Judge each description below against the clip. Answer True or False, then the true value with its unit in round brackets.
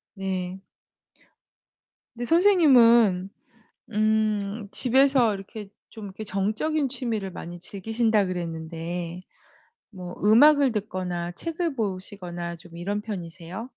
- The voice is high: True (205 Hz)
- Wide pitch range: False (4.4 semitones)